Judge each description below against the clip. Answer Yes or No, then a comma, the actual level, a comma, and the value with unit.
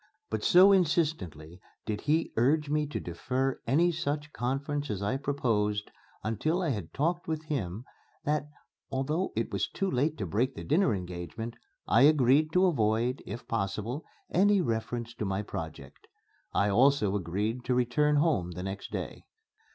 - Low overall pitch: Yes, low, 125 Hz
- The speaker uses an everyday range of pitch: No, wide, 6.5 semitones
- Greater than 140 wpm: Yes, average, 160 wpm